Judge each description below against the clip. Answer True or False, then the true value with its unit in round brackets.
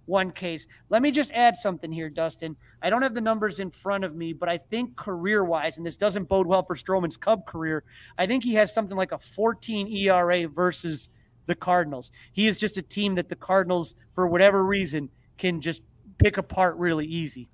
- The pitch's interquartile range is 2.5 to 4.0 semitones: True (3.7 semitones)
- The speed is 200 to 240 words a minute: True (205 wpm)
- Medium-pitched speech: True (180 Hz)